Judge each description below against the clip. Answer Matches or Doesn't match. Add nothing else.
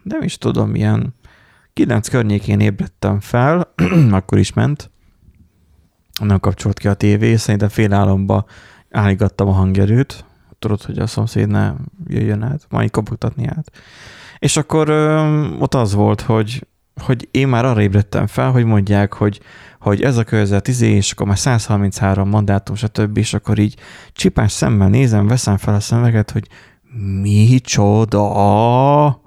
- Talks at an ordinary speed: Matches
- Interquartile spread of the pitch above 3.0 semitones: Matches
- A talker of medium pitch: Doesn't match